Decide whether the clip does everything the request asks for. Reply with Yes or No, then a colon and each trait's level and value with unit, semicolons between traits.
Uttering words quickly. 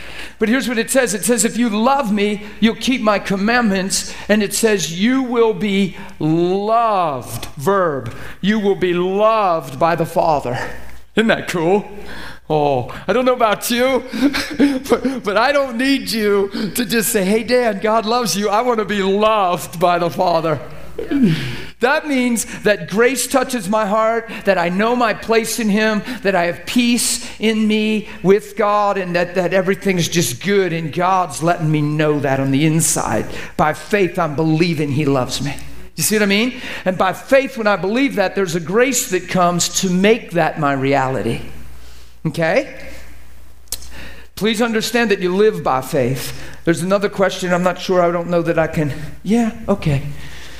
No: average, 175 wpm